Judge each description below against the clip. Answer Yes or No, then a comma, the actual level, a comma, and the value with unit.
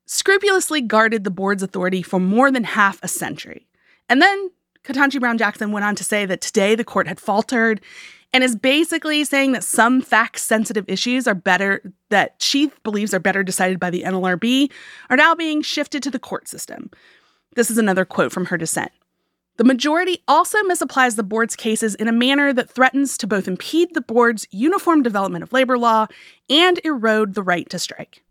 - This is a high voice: Yes, high, 230 Hz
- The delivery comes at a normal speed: Yes, average, 180 wpm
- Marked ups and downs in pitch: Yes, wide, 5.9 semitones